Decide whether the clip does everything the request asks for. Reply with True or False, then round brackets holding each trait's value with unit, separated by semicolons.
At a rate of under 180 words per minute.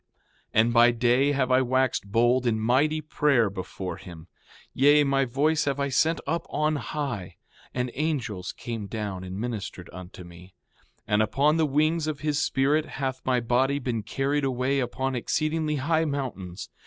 True (170 wpm)